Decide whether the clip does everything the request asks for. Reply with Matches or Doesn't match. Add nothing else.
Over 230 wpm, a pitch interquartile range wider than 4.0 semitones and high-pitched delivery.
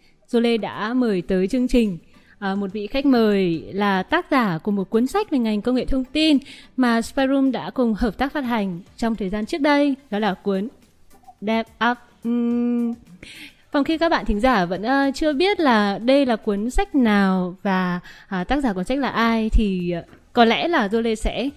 Doesn't match